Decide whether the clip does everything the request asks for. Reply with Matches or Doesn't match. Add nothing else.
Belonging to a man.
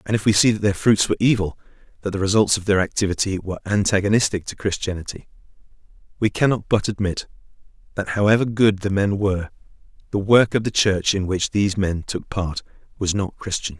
Matches